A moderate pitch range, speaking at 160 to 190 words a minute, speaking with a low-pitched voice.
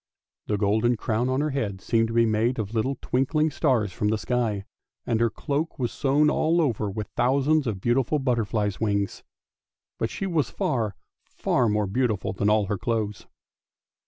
Yes: average, 4.1 semitones; average, 180 wpm; low, 115 Hz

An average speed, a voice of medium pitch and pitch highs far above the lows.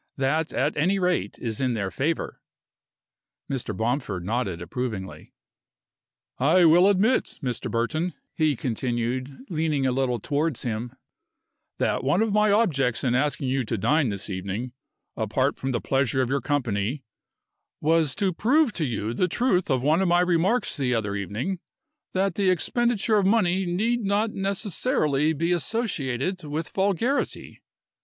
Yes: average, 150 wpm; medium, 150 Hz; wide, 7.1 semitones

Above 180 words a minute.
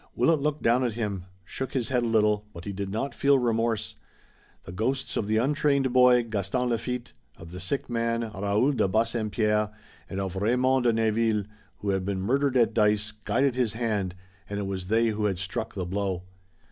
Yes: average, 195 wpm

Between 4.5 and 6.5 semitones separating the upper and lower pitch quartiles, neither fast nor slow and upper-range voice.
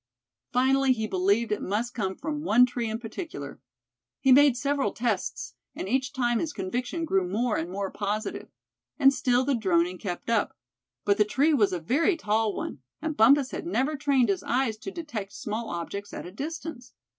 Yes: average, 4.9 semitones; average, 185 wpm; high, 240 Hz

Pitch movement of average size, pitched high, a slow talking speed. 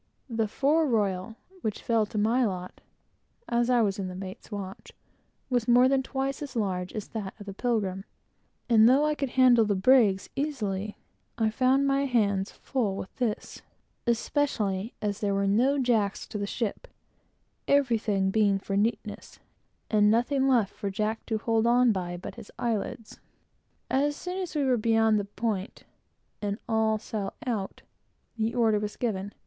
No: average, 3.7 semitones; high, 220 Hz; average, 170 wpm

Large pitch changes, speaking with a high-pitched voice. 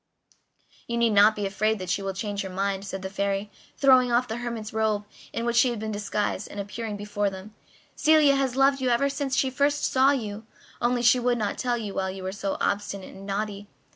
No: average, 3.5 semitones; high, 215 Hz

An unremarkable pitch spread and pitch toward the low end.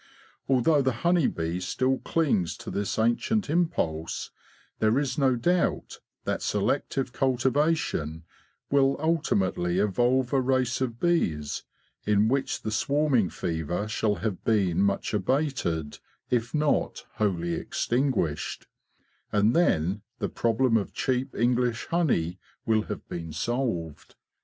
No: wide, 6.4 semitones; low, 120 Hz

